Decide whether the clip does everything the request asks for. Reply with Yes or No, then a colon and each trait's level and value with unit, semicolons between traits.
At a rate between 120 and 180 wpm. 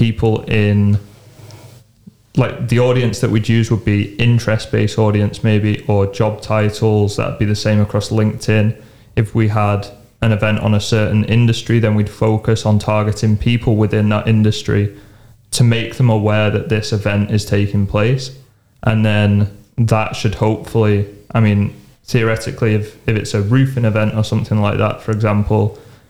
Yes: average, 165 wpm